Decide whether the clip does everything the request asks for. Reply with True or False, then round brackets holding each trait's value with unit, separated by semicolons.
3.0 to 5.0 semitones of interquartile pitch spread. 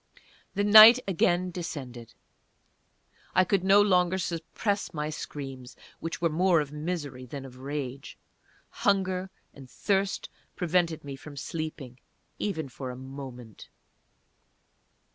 False (5.5 semitones)